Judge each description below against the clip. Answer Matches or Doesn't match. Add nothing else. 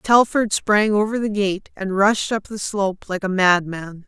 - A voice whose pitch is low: Doesn't match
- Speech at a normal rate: Matches